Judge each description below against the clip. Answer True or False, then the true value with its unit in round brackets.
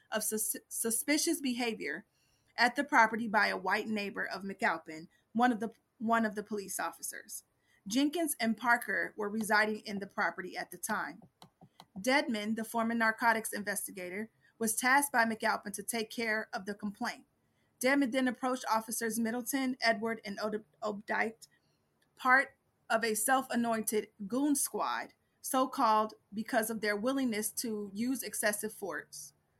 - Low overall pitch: False (225 Hz)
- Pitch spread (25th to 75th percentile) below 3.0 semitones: True (2.6 semitones)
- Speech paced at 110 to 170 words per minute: True (140 wpm)